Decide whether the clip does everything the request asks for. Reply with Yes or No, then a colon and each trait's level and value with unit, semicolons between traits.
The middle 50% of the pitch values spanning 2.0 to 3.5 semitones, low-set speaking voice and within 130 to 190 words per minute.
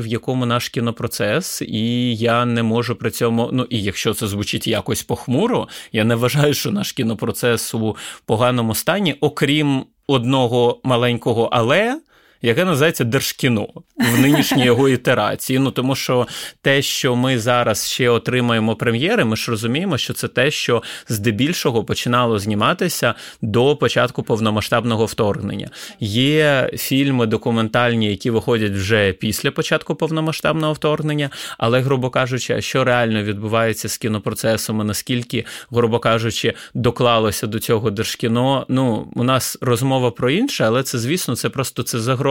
Yes: average, 2.9 semitones; low, 120 Hz; average, 140 wpm